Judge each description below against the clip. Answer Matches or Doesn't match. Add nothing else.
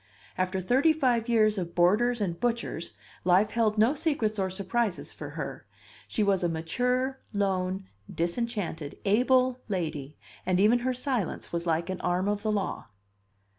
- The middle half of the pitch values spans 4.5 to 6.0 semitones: Matches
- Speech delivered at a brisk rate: Doesn't match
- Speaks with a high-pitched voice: Matches